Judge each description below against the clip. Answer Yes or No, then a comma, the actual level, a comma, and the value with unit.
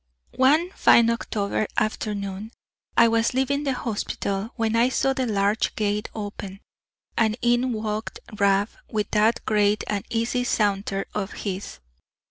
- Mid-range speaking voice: No, high, 215 Hz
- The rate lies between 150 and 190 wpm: No, slow, 135 wpm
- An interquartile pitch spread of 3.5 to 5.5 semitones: No, narrow, 2.5 semitones